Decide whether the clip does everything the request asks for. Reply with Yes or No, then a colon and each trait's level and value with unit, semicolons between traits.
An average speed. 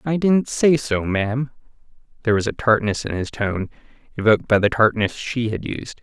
Yes: average, 190 wpm